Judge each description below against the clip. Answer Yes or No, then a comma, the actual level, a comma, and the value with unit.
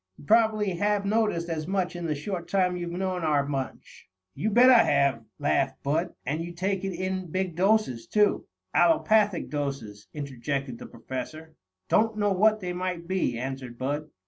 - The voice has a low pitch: No, medium, 175 Hz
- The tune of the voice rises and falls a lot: Yes, wide, 5.8 semitones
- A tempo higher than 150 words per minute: Yes, average, 170 wpm